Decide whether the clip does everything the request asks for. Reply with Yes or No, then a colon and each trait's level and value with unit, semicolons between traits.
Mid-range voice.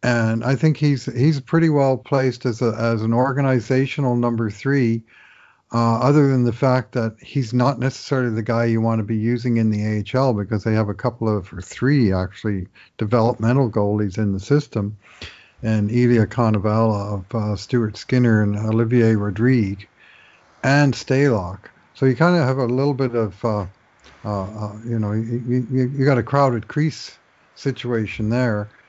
No: low, 115 Hz